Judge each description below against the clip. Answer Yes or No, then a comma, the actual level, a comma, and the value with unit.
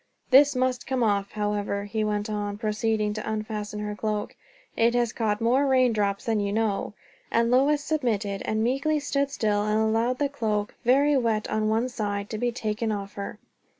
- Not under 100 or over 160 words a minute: No, average, 185 wpm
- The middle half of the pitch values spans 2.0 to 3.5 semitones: Yes, average, 3.1 semitones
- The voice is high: Yes, high, 220 Hz